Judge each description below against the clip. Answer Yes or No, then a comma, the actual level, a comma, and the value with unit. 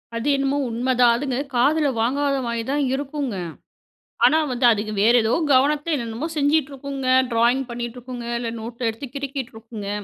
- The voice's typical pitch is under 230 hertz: No, very high, 255 Hz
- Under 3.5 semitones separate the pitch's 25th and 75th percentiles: Yes, average, 3.0 semitones